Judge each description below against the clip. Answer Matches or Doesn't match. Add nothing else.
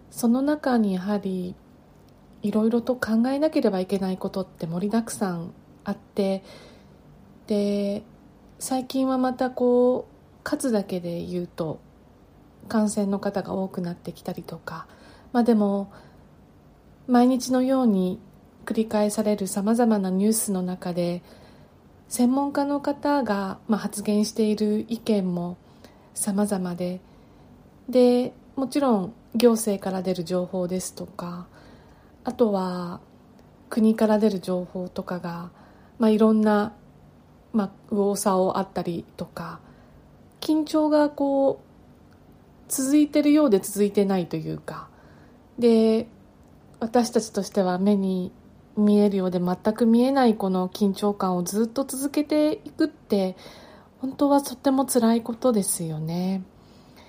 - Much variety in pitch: Doesn't match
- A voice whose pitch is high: Matches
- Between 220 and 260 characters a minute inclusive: Matches